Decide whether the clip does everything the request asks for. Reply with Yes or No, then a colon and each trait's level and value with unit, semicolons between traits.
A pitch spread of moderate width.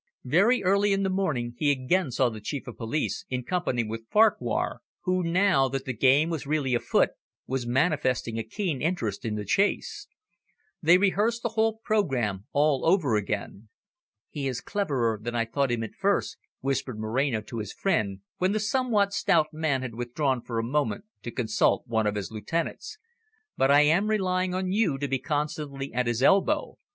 No: wide, 7.6 semitones